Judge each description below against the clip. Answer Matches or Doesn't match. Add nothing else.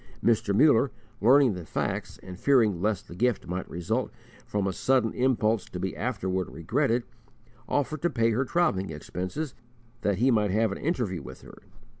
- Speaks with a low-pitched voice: Matches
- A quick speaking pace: Doesn't match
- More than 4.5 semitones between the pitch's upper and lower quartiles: Matches